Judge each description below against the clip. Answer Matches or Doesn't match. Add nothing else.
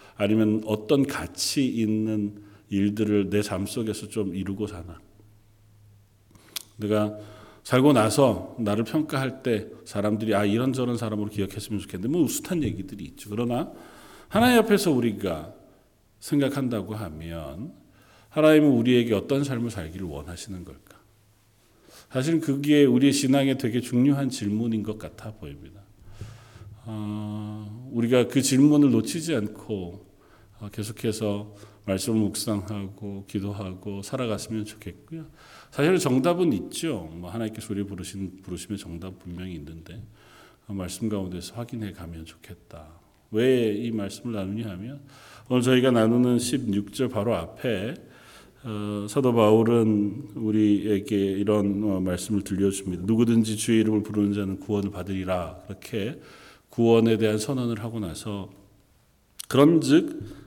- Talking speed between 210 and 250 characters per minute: Doesn't match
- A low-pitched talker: Matches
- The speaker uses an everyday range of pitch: Matches